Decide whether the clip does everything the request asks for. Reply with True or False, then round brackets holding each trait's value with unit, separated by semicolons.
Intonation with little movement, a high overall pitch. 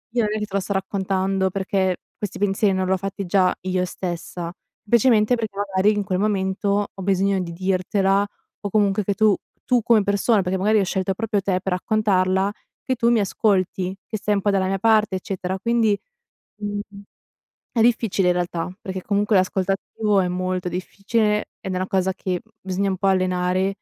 True (1.9 semitones; 195 Hz)